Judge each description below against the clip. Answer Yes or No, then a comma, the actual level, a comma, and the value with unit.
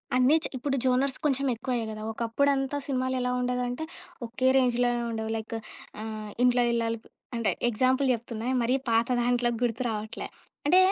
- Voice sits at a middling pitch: No, high, 245 Hz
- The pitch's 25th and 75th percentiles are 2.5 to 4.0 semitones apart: No, narrow, 2.1 semitones